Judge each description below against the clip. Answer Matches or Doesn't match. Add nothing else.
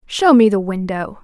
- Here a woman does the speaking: Matches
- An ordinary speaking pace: Matches